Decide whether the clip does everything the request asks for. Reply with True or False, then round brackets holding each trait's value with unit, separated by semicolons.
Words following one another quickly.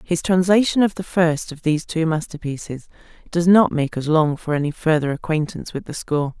False (195 wpm)